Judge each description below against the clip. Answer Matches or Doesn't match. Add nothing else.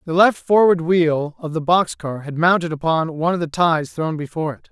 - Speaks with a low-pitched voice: Doesn't match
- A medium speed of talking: Doesn't match